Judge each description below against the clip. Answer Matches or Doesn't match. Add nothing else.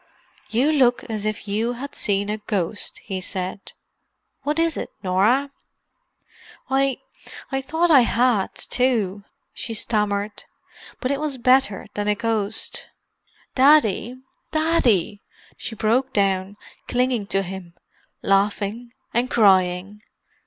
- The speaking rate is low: Matches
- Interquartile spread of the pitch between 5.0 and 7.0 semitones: Doesn't match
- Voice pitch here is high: Matches